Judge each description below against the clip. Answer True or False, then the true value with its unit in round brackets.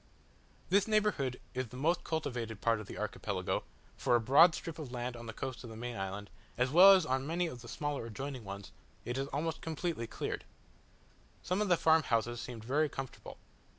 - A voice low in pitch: True (130 Hz)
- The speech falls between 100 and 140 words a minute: False (195 wpm)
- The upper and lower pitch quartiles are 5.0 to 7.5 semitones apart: True (5.5 semitones)